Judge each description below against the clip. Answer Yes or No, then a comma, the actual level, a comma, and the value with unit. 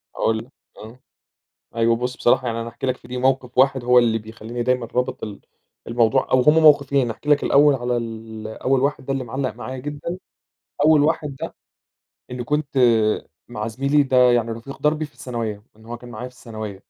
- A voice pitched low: Yes, low, 125 Hz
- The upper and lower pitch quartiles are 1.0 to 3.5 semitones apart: Yes, average, 3.0 semitones